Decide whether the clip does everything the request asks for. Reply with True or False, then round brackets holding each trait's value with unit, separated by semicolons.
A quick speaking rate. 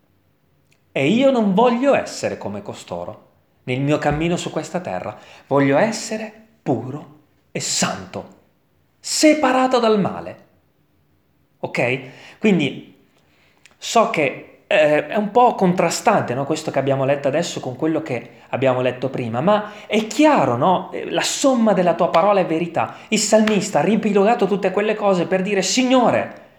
False (140 wpm)